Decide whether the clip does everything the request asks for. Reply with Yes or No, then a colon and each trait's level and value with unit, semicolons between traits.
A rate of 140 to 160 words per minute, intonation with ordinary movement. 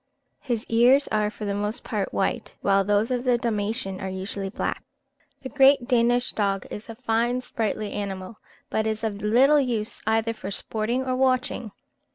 No: average, 175 wpm; average, 3.1 semitones